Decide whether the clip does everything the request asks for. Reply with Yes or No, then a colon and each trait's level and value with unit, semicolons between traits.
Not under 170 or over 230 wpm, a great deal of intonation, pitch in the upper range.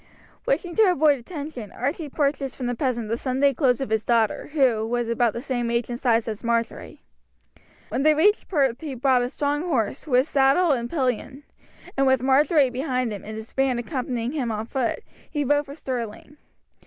No: average, 190 wpm; average, 3.4 semitones; very high, 260 Hz